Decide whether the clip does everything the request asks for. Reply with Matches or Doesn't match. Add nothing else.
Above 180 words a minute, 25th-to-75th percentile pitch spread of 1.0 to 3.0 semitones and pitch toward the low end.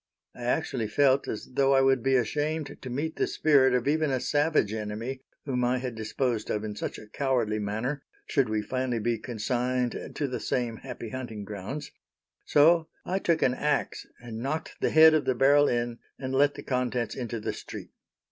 Doesn't match